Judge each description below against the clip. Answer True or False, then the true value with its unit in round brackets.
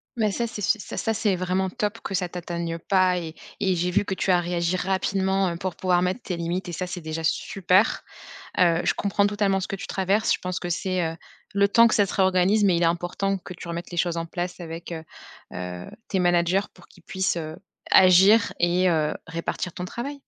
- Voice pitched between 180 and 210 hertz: True (185 Hz)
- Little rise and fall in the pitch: True (2.3 semitones)